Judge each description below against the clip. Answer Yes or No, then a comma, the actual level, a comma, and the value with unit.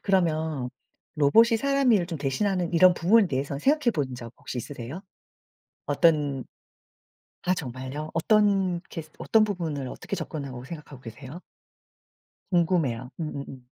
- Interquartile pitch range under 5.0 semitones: No, wide, 5.4 semitones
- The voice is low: No, medium, 160 Hz